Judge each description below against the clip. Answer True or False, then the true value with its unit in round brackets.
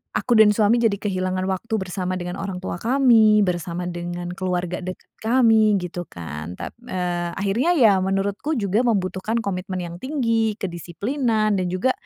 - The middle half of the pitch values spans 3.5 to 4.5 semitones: True (3.8 semitones)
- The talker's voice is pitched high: True (195 Hz)